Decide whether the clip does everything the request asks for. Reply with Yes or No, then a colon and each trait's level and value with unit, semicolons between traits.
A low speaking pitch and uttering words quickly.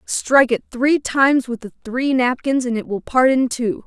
No: very high, 250 Hz; fast, 215 wpm